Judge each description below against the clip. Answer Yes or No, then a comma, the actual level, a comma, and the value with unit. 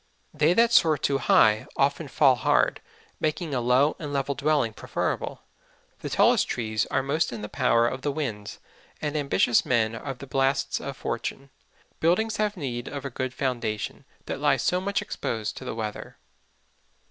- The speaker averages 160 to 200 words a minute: Yes, average, 170 wpm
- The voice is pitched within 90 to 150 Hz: Yes, low, 135 Hz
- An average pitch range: Yes, average, 4.3 semitones